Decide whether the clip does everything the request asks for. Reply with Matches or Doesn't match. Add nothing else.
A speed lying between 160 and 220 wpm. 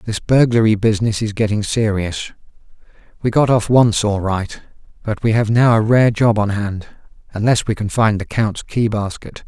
Matches